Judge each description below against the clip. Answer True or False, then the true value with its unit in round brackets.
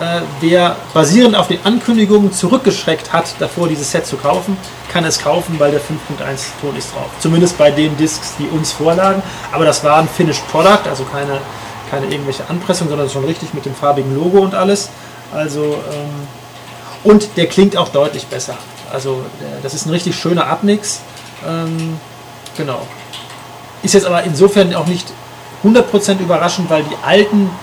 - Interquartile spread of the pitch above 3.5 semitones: True (4.4 semitones)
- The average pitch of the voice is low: False (160 Hz)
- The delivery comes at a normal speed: True (165 wpm)